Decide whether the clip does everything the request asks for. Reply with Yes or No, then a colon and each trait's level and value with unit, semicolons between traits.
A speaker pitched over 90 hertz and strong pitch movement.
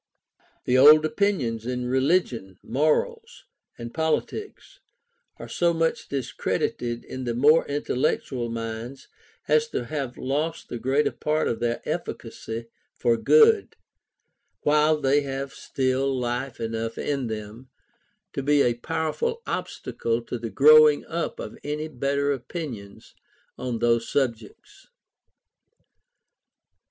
No: low, 135 Hz; average, 4.5 semitones